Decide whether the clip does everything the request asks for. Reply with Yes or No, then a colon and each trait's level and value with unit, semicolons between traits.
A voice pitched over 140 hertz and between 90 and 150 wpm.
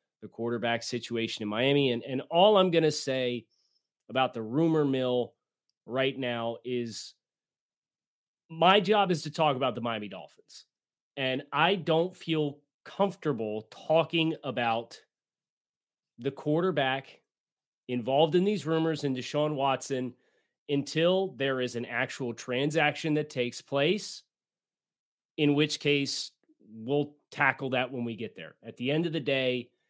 No: low, 135 Hz; average, 140 wpm